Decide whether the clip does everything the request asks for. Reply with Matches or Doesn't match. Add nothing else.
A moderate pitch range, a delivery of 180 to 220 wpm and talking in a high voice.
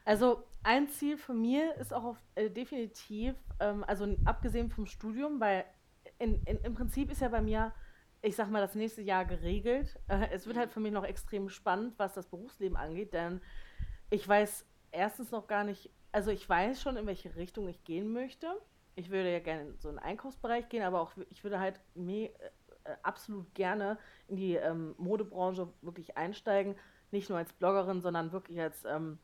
Matches